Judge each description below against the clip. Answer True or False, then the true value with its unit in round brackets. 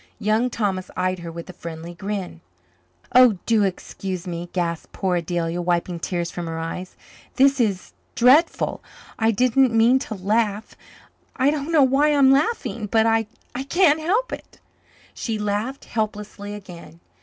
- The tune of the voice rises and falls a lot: True (6.0 semitones)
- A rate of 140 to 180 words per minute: True (150 wpm)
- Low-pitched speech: False (210 Hz)